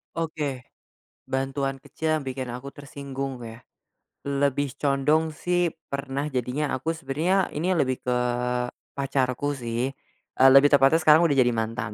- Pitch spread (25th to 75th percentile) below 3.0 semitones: Yes, narrow, 2.6 semitones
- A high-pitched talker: No, medium, 140 Hz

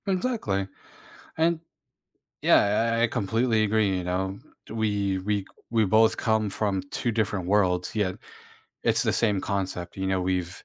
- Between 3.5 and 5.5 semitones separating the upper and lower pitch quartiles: No, narrow, 2.6 semitones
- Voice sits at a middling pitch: No, low, 100 Hz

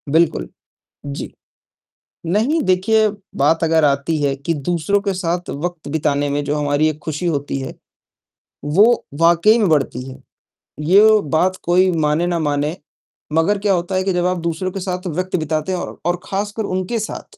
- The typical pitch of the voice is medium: Yes, medium, 175 Hz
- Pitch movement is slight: No, average, 3.9 semitones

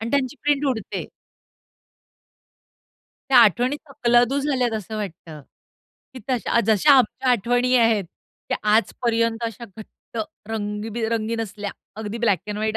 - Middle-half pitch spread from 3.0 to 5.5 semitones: No, narrow, 2.5 semitones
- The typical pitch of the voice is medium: No, high, 230 Hz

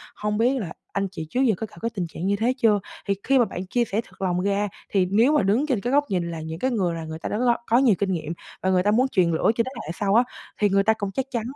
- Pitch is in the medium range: No, high, 205 Hz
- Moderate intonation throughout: Yes, average, 4.4 semitones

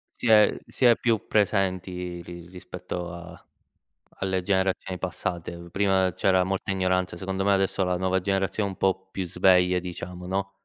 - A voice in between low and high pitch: No, very low, 95 Hz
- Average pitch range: No, narrow, 1.3 semitones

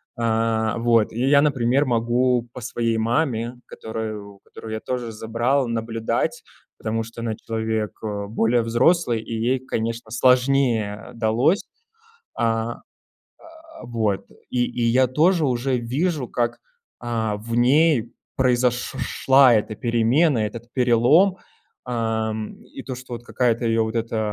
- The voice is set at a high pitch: No, low, 120 Hz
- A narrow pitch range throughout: Yes, narrow, 2.2 semitones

